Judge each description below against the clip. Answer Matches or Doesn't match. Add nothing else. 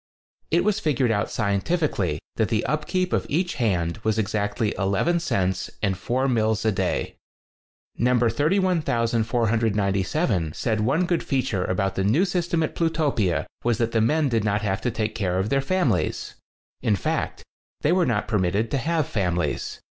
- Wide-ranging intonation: Matches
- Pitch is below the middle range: Matches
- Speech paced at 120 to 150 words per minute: Doesn't match